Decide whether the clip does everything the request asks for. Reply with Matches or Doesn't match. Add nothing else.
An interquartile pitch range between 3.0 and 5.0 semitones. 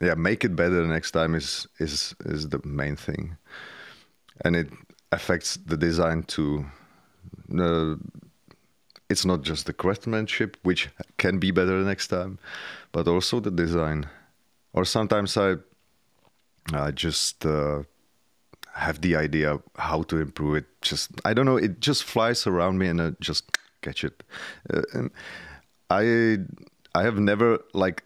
Matches